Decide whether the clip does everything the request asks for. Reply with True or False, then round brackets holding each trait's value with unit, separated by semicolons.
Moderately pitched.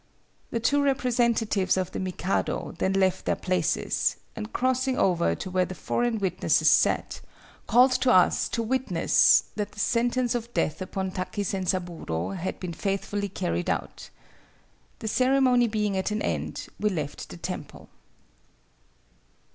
False (200 Hz)